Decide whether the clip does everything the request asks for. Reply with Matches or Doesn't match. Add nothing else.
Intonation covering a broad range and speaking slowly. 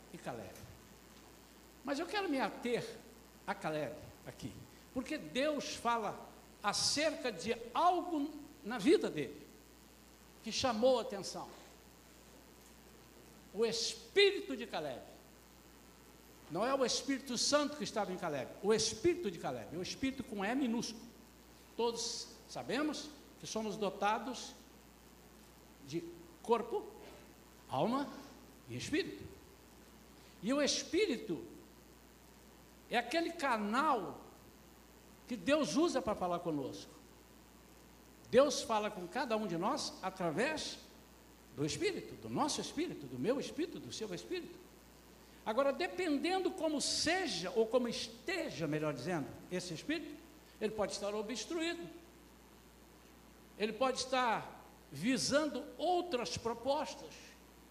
Matches